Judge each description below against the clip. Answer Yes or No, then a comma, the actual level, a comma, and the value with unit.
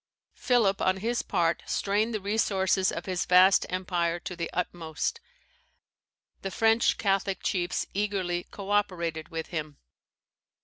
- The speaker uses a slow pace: Yes, slow, 130 wpm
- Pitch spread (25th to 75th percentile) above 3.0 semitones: No, average, 2.7 semitones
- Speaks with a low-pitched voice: No, medium, 185 Hz